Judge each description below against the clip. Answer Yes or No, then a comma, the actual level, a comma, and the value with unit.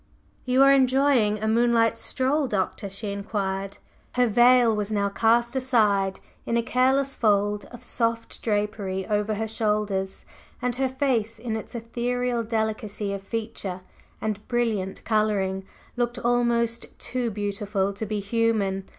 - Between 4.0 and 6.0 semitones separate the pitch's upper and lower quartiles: No, average, 3.0 semitones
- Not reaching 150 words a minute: Yes, average, 140 wpm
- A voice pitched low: No, high, 220 Hz